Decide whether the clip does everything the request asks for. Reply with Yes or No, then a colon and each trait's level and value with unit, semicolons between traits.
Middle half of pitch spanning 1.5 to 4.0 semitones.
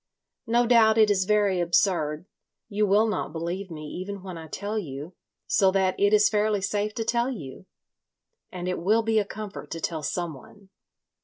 Yes: average, 3.4 semitones